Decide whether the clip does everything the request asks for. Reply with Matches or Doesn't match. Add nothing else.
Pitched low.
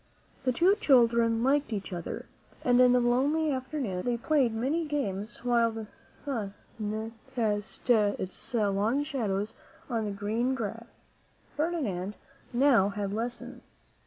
Doesn't match